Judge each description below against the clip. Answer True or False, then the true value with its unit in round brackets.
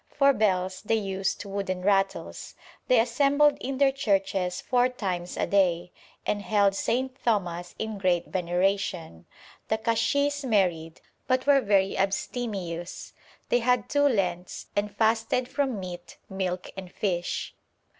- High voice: True (200 Hz)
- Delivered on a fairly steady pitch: False (5.1 semitones)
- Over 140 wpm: False (135 wpm)